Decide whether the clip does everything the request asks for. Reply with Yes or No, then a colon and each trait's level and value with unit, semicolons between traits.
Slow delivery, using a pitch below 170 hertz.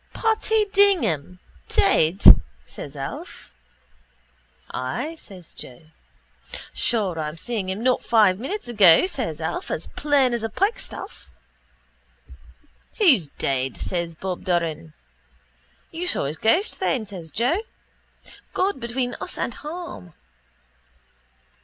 No: slow, 115 wpm; high, 220 Hz